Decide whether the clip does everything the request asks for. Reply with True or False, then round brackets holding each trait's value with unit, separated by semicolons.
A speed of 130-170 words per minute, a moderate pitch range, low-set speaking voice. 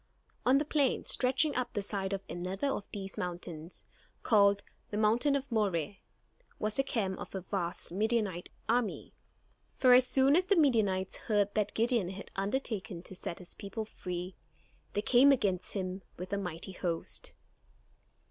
False (160 wpm; 4.6 semitones; 205 Hz)